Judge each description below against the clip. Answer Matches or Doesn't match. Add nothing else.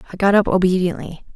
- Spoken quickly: Doesn't match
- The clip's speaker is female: Matches